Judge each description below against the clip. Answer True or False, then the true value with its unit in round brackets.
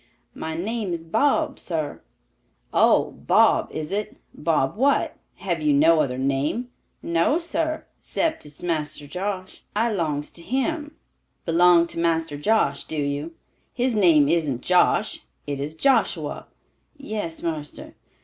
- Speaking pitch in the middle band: True (170 Hz)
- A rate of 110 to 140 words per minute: True (135 wpm)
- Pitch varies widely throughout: True (6.2 semitones)